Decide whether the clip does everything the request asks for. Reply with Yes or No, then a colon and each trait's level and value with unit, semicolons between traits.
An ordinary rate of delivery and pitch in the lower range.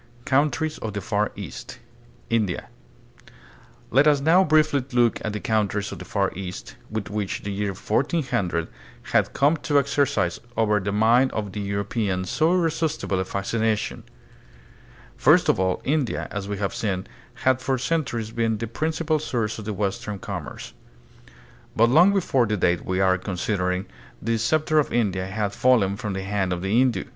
Yes: average, 170 wpm; low, 110 Hz